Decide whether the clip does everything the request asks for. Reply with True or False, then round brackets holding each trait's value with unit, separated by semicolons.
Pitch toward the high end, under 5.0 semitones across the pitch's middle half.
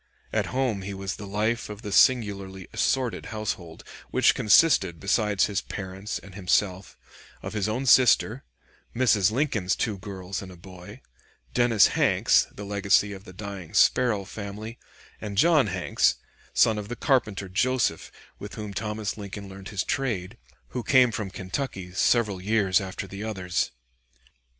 False (100 Hz; 2.7 semitones)